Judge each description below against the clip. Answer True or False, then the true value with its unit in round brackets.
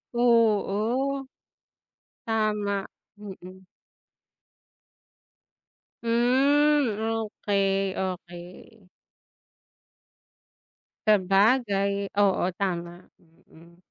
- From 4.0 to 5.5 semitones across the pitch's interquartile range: False (3.4 semitones)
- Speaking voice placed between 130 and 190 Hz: False (205 Hz)